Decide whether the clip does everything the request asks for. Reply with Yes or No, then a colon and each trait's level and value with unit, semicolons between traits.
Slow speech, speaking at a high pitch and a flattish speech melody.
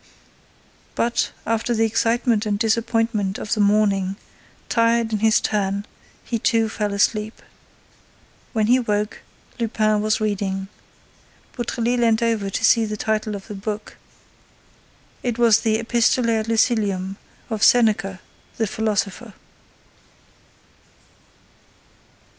Yes: slow, 115 wpm; high, 220 Hz; narrow, 1.8 semitones